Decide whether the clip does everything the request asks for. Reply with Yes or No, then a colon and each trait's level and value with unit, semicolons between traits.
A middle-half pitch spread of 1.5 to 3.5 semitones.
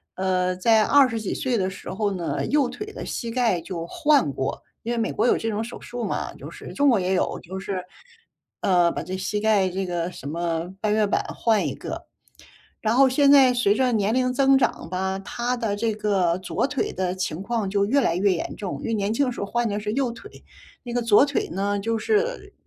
No: average, 4.6 semitones